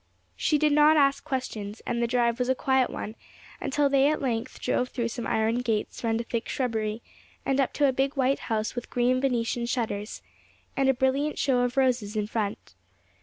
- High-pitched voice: Yes, high, 245 Hz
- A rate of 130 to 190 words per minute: No, average, 200 wpm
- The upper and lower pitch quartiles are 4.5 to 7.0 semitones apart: No, average, 3.0 semitones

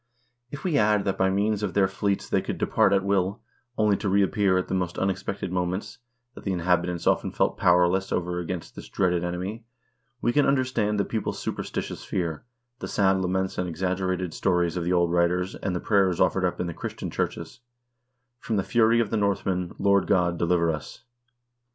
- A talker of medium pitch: No, very low, 95 Hz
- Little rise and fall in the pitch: Yes, narrow, 2.2 semitones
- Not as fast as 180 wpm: No, average, 195 wpm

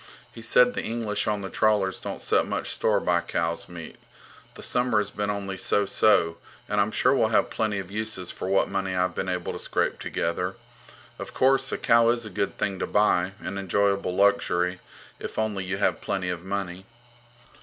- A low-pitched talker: Yes, low, 100 Hz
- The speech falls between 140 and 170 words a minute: No, average, 195 wpm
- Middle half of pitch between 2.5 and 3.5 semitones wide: Yes, average, 2.8 semitones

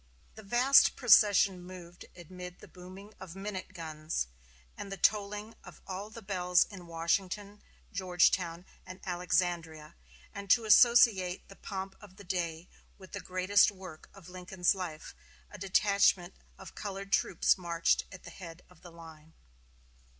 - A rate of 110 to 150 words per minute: Yes, average, 145 wpm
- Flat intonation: Yes, narrow, 2.3 semitones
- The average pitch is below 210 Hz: Yes, medium, 185 Hz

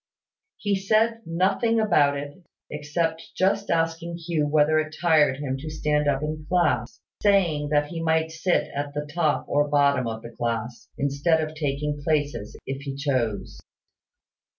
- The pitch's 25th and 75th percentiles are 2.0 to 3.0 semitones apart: Yes, average, 2.7 semitones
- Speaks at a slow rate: No, average, 155 wpm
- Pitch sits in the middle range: Yes, medium, 150 Hz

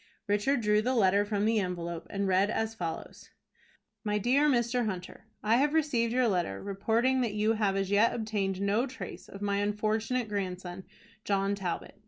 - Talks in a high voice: Yes, high, 210 Hz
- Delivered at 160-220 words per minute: Yes, average, 175 wpm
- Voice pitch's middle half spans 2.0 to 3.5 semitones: Yes, average, 2.9 semitones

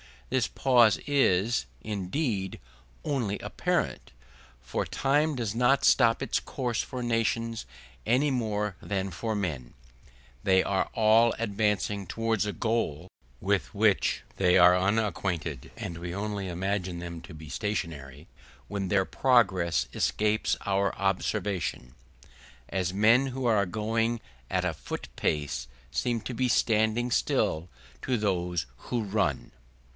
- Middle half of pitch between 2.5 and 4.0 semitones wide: No, average, 4.4 semitones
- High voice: No, low, 105 Hz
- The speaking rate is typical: No, slow, 130 wpm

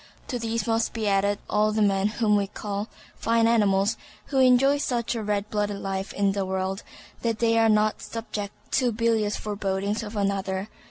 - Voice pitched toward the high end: Yes, high, 210 Hz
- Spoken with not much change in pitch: Yes, narrow, 2.3 semitones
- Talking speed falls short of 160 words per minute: No, average, 180 wpm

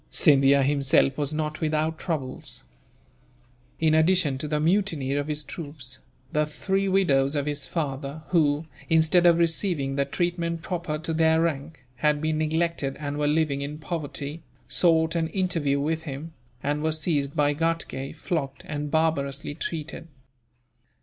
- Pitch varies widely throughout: No, narrow, 2.4 semitones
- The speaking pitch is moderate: Yes, medium, 155 Hz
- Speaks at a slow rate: No, average, 150 wpm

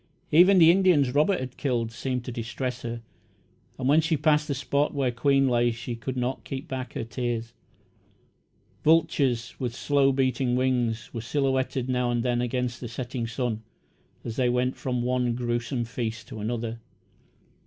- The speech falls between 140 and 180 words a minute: Yes, average, 165 wpm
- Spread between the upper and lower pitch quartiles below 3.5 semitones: Yes, narrow, 2.4 semitones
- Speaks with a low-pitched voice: Yes, low, 125 Hz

